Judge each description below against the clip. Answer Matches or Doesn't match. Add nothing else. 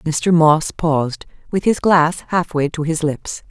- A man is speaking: Doesn't match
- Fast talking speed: Doesn't match